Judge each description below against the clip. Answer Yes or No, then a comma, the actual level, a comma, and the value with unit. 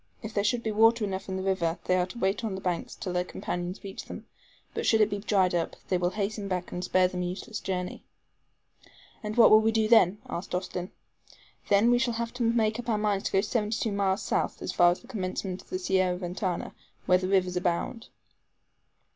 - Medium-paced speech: No, fast, 225 wpm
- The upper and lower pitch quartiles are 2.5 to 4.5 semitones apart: Yes, average, 3.1 semitones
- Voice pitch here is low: No, high, 195 Hz